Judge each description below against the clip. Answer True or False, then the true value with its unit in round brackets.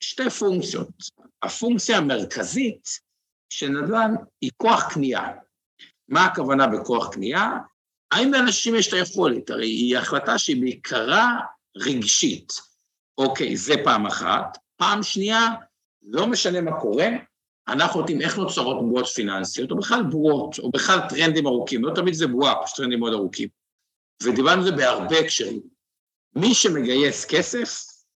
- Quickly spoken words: False (135 wpm)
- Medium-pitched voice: True (180 Hz)